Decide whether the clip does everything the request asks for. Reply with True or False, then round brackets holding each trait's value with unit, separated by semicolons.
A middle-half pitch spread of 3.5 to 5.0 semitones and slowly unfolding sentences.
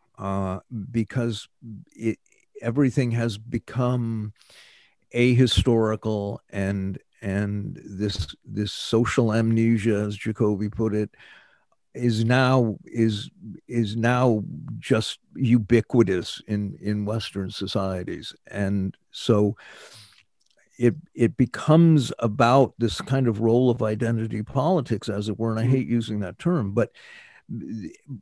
False (2.7 semitones; 110 wpm)